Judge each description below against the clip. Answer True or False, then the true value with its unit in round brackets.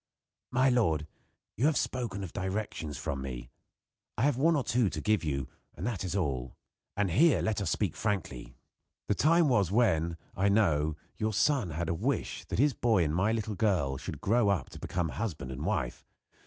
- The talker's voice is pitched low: True (100 Hz)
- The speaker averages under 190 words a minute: False (195 wpm)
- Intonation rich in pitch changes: True (6.4 semitones)